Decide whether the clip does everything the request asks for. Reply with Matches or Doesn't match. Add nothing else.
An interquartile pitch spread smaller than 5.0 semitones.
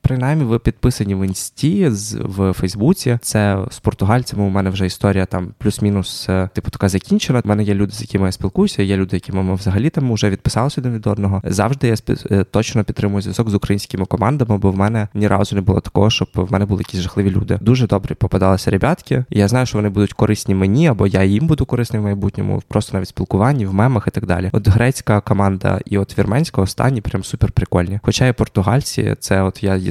Matches